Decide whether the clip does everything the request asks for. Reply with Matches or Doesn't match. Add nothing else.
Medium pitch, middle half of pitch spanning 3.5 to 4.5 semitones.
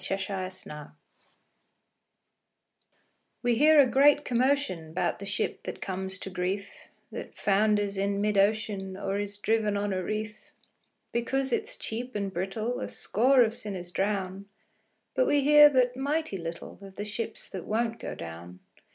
Doesn't match